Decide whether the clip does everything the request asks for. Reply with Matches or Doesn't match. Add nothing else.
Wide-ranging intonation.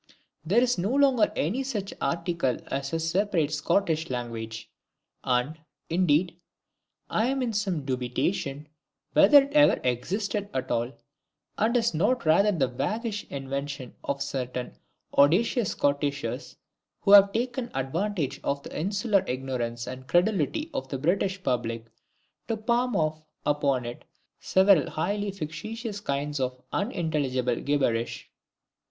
Matches